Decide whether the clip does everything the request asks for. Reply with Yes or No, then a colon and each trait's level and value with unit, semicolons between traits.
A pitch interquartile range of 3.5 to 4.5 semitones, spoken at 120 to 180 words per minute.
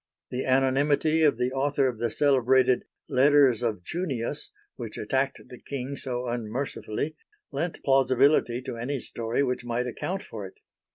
No: average, 2.8 semitones; average, 150 wpm